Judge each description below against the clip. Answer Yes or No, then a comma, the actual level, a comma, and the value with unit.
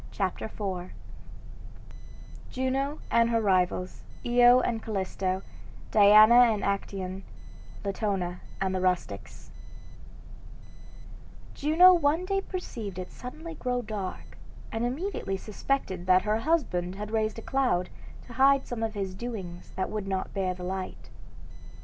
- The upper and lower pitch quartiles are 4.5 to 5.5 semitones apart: Yes, average, 4.8 semitones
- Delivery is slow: Yes, slow, 125 wpm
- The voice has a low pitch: No, high, 215 Hz